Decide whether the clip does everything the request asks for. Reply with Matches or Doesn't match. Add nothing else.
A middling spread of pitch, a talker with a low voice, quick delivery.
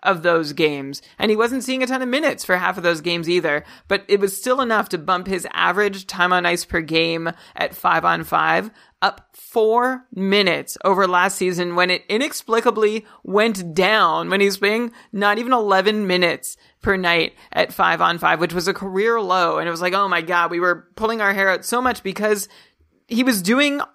Doesn't match